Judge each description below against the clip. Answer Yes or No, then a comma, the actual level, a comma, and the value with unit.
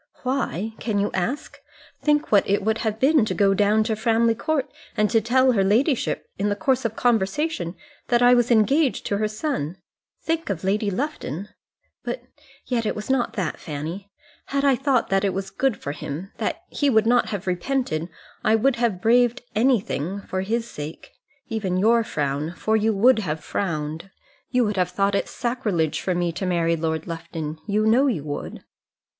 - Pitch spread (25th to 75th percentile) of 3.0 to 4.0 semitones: No, average, 4.9 semitones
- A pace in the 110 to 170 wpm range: No, average, 185 wpm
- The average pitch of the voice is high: Yes, high, 215 Hz